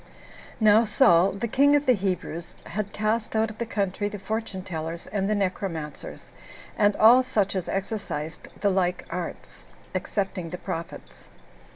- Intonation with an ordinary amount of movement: Yes, average, 3.2 semitones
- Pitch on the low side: No, high, 200 Hz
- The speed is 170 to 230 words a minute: No, average, 160 wpm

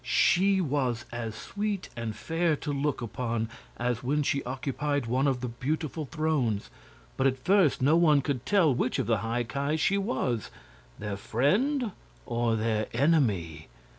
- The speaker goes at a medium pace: Yes, average, 160 wpm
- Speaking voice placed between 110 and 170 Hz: Yes, low, 135 Hz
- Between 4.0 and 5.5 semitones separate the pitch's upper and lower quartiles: Yes, average, 5.1 semitones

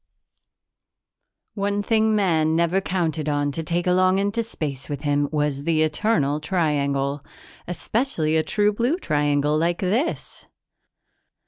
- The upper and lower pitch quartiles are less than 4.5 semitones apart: No, average, 5.3 semitones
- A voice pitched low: No, medium, 160 Hz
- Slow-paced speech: Yes, slow, 125 wpm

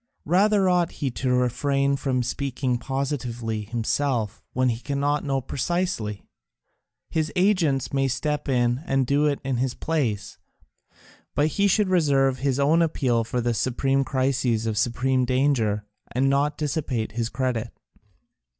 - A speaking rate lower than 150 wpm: Yes, average, 140 wpm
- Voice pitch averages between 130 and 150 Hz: Yes, low, 135 Hz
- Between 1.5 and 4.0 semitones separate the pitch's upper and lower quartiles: Yes, average, 3.1 semitones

